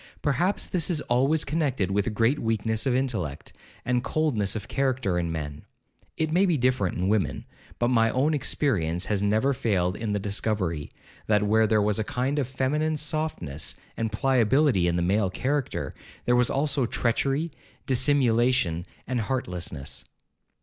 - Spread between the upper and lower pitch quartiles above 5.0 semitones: Yes, wide, 5.4 semitones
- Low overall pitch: Yes, low, 120 Hz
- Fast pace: No, average, 155 wpm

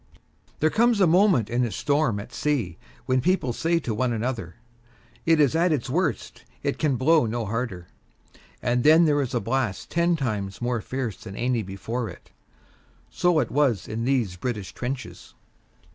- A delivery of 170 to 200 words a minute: Yes, average, 175 wpm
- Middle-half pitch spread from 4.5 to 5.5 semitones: Yes, average, 5.2 semitones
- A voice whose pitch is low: Yes, low, 125 Hz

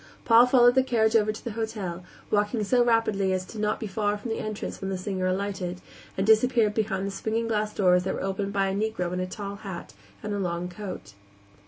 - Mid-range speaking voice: No, high, 205 Hz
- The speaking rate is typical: No, fast, 225 wpm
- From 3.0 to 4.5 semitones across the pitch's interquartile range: No, narrow, 2.5 semitones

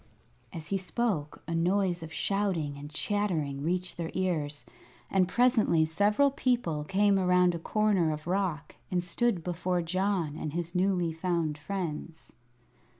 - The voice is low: No, medium, 180 Hz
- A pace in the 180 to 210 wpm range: No, average, 145 wpm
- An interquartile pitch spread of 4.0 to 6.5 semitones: No, average, 3.5 semitones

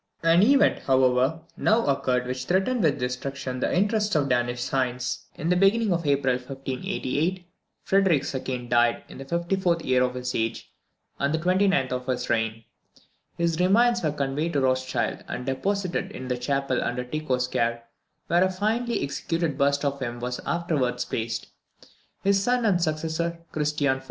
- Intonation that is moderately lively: No, wide, 5.7 semitones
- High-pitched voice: No, medium, 140 Hz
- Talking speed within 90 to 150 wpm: No, average, 165 wpm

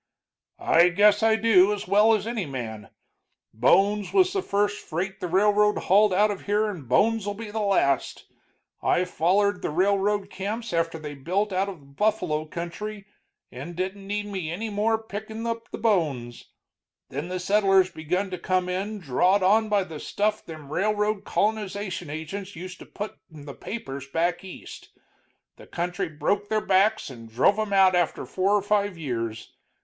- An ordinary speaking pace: Yes, average, 175 wpm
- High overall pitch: Yes, high, 195 Hz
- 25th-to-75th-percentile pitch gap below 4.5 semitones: Yes, average, 3.7 semitones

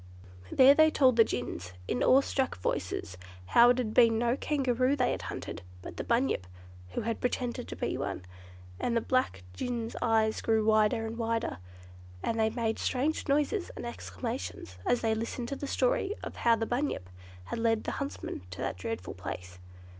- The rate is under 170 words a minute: No, average, 185 wpm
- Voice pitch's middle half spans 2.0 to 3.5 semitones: Yes, average, 2.7 semitones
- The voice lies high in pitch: Yes, high, 235 Hz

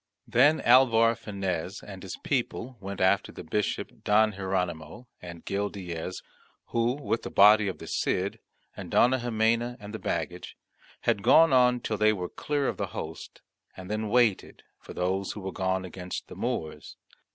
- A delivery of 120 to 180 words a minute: Yes, average, 170 wpm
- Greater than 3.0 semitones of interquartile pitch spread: Yes, average, 3.9 semitones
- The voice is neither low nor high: No, low, 105 Hz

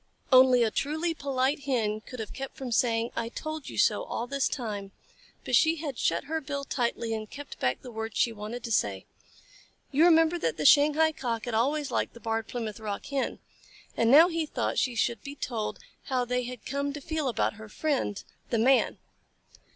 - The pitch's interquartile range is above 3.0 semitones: Yes, average, 4.3 semitones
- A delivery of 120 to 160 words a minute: No, average, 200 wpm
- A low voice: No, very high, 250 Hz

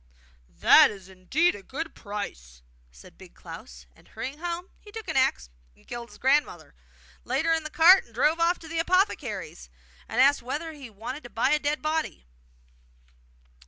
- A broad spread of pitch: Yes, wide, 7.7 semitones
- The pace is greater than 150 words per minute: Yes, average, 180 wpm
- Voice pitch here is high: Yes, very high, 275 Hz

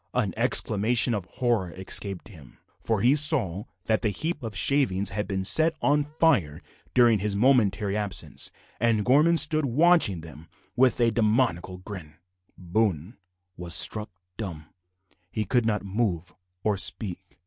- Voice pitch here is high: No, low, 105 Hz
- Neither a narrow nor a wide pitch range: Yes, average, 4.8 semitones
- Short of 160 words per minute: Yes, average, 145 wpm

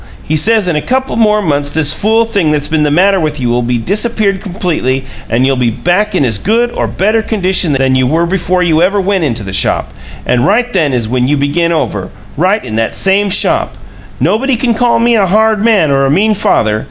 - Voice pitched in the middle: Yes, medium, 175 Hz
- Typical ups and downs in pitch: No, wide, 7.5 semitones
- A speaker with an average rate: No, fast, 225 wpm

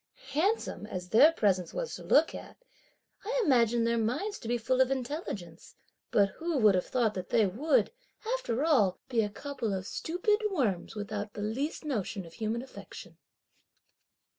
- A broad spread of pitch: Yes, wide, 6.4 semitones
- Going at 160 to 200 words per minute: Yes, average, 165 wpm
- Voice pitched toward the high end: Yes, high, 235 Hz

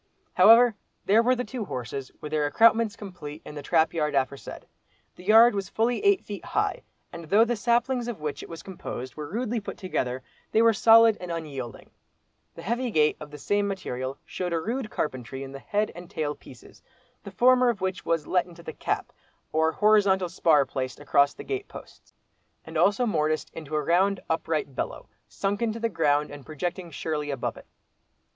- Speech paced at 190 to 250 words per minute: Yes, average, 195 wpm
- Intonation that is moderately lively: No, wide, 6.8 semitones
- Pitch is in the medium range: Yes, medium, 175 Hz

